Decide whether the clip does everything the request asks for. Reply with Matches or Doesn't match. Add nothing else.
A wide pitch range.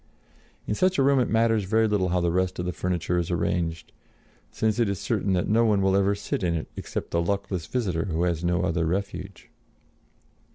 Doesn't match